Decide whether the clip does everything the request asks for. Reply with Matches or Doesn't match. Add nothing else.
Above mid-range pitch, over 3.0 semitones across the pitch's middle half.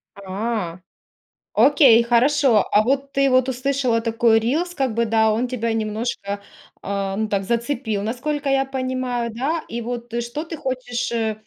Matches